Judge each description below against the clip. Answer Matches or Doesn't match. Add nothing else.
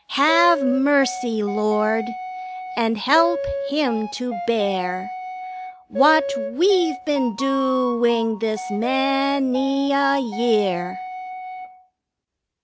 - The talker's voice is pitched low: Doesn't match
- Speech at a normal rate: Doesn't match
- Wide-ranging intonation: Doesn't match